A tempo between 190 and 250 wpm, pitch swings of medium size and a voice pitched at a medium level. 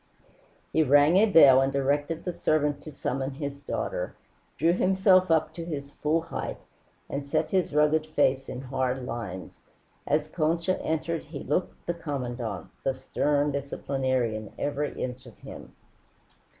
No: average, 150 wpm; average, 3.3 semitones; medium, 145 Hz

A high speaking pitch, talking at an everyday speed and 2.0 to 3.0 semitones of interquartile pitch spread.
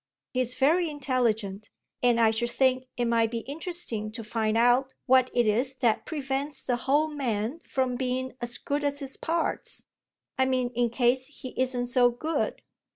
Yes: very high, 255 Hz; average, 170 wpm; narrow, 2.4 semitones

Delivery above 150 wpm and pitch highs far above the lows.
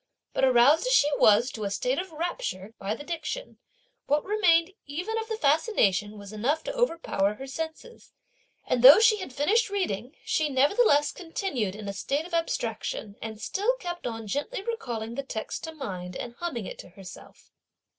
Yes: average, 180 wpm; wide, 8.5 semitones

